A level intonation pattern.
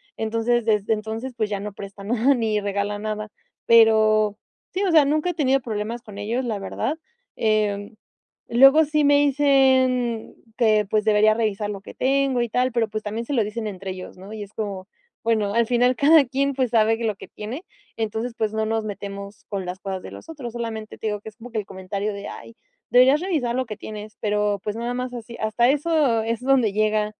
No: average, 3.1 semitones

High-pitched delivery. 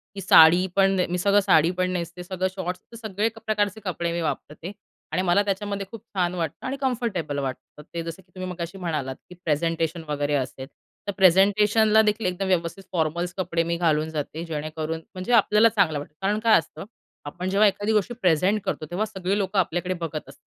No: medium, 180 Hz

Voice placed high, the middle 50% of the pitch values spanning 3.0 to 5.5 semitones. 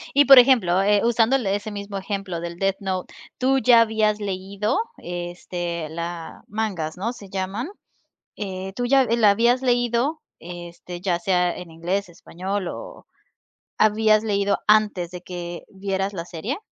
Yes: high, 195 Hz; average, 3.9 semitones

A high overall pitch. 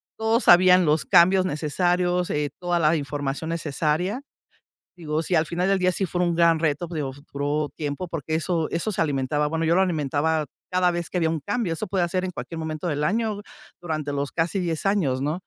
No: medium, 165 Hz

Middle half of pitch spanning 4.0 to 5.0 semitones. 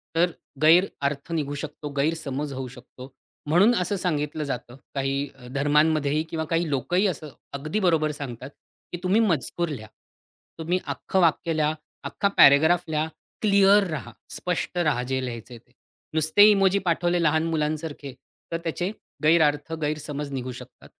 No: average, 3.5 semitones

